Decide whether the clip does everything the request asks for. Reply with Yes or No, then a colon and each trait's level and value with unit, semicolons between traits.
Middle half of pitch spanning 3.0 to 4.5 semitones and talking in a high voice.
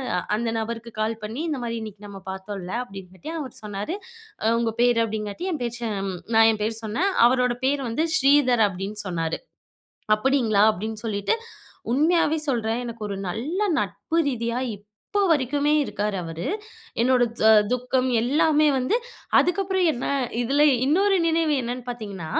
No: average, 5.0 semitones; high, 235 Hz